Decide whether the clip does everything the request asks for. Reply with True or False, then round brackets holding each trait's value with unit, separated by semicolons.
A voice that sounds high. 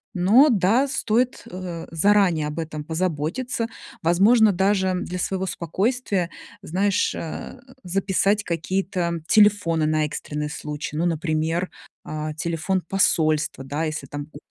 False (175 Hz)